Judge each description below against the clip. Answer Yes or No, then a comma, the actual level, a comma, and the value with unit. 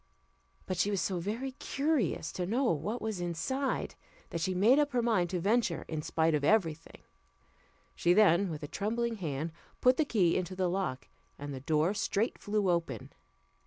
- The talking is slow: No, average, 185 wpm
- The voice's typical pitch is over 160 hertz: Yes, medium, 185 Hz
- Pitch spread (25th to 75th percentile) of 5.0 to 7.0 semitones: Yes, average, 5.3 semitones